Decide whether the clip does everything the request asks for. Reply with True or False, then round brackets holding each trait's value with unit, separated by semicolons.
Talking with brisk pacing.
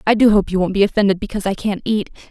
True (285 wpm)